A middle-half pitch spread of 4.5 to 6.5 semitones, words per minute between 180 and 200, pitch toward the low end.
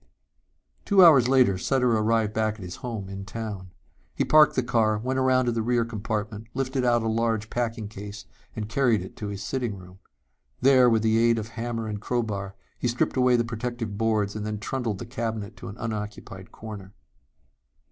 No: average, 2.7 semitones; average, 190 wpm; low, 115 Hz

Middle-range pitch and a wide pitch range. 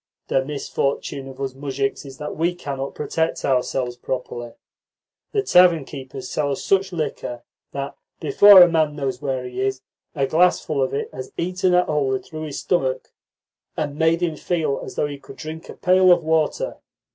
No: medium, 145 Hz; average, 3.8 semitones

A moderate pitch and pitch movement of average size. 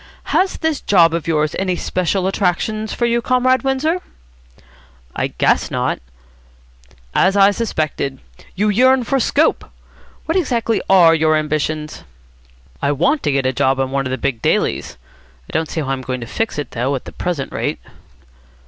No: medium, 175 Hz; wide, 8.7 semitones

